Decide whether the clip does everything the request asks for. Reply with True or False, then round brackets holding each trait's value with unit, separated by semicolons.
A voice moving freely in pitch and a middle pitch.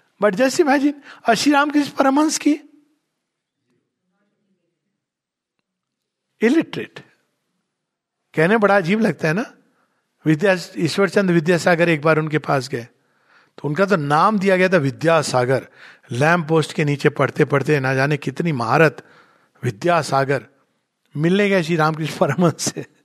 True (5.8 semitones; 170 Hz)